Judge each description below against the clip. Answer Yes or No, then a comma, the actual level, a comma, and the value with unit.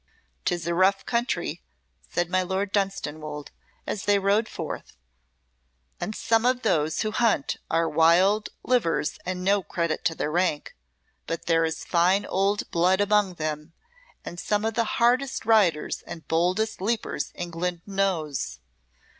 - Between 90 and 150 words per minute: Yes, average, 145 wpm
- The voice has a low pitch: No, medium, 185 Hz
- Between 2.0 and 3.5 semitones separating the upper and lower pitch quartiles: No, average, 3.9 semitones